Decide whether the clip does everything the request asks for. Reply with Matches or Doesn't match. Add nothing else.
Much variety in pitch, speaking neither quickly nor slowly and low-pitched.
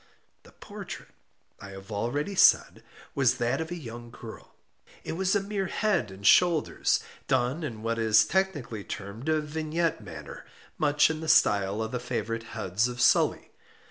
Matches